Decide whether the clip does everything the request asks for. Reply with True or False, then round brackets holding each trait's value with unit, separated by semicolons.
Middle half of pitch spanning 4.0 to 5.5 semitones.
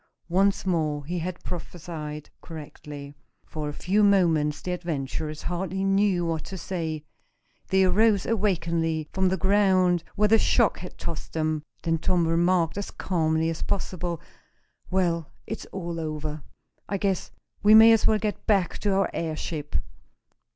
False (3.4 semitones)